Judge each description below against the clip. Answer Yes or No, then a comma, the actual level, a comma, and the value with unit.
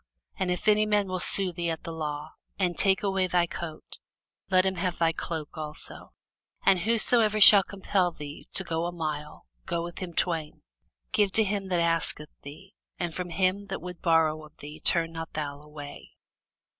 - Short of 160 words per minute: No, average, 185 wpm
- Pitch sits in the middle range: Yes, medium, 175 Hz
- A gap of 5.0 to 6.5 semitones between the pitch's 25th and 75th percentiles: No, average, 3.1 semitones